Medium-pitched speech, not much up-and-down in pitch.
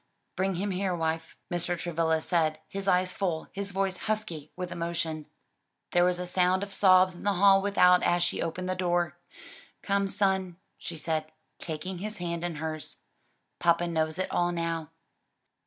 Yes: medium, 175 Hz; narrow, 2.3 semitones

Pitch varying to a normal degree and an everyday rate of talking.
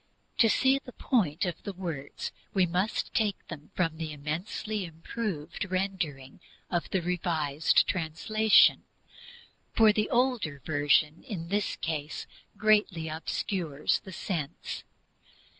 No: average, 5.0 semitones; slow, 120 wpm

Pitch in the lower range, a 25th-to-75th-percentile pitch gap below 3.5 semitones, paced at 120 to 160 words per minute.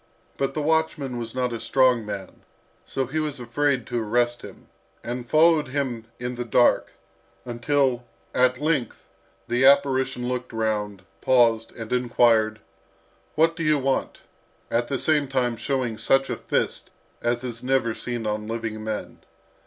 Yes: low, 125 Hz; average, 2.8 semitones; average, 155 wpm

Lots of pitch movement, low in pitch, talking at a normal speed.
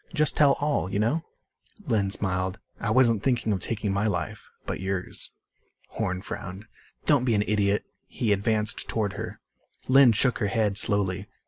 No: average, 2.9 semitones; low, 105 Hz; average, 160 wpm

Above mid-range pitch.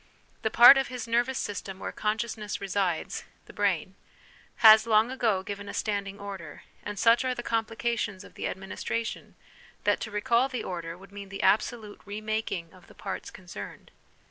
Yes: high, 210 Hz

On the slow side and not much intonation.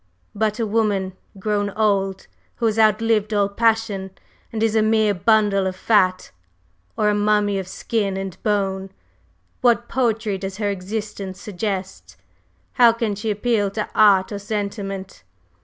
No: average, 145 wpm; narrow, 2.0 semitones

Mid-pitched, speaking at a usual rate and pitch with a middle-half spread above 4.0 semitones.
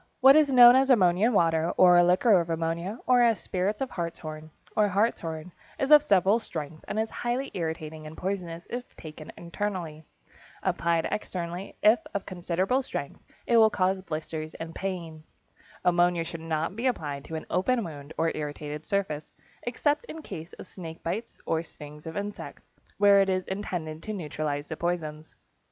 Yes: medium, 175 Hz; average, 170 wpm; average, 4.6 semitones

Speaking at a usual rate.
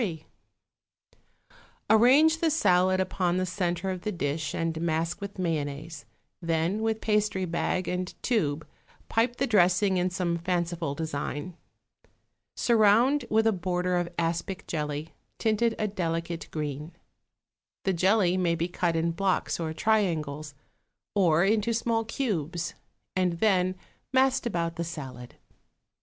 No: slow, 130 wpm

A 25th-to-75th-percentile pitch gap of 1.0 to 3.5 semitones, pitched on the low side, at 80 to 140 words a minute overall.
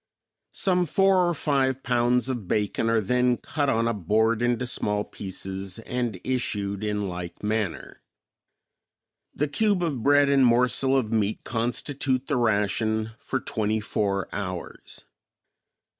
No: average, 4.1 semitones; low, 115 Hz; slow, 135 wpm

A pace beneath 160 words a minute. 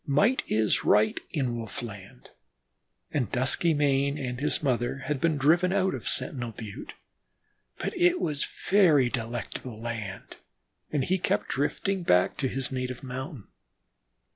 Yes: average, 140 wpm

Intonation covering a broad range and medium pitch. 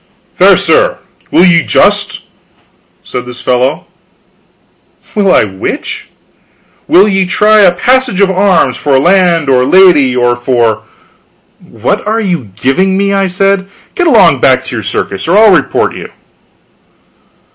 Yes: wide, 7.4 semitones; medium, 180 Hz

